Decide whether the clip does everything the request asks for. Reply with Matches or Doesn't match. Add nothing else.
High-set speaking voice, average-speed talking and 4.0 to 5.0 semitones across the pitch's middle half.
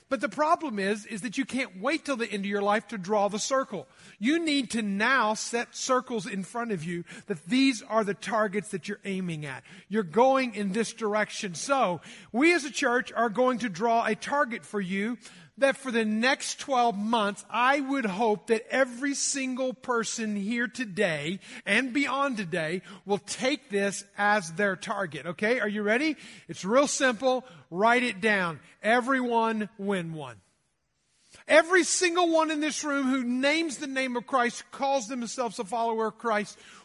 Matches